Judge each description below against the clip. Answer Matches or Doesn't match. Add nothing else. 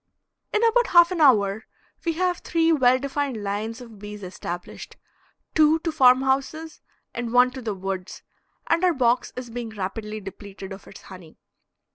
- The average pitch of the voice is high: Matches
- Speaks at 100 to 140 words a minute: Doesn't match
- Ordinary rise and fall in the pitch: Doesn't match